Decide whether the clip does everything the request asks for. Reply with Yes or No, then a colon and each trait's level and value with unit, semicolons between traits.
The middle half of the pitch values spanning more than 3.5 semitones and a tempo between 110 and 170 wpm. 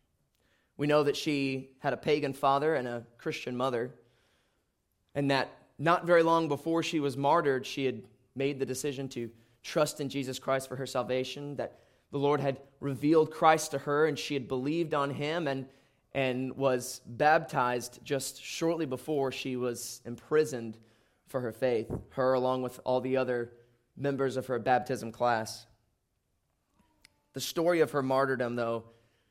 No: average, 2.7 semitones; average, 160 wpm